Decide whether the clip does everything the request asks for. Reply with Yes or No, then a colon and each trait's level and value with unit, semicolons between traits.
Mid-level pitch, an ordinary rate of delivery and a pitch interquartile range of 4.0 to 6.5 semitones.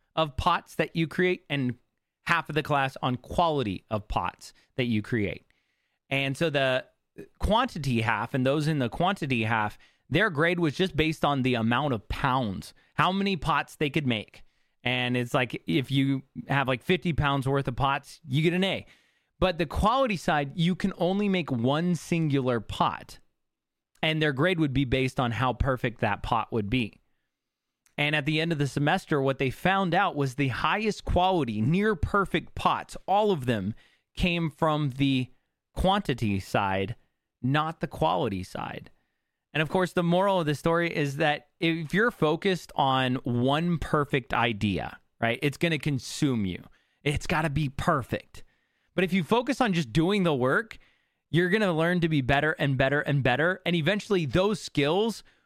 Yes: medium, 145 Hz; average, 175 wpm; average, 5.1 semitones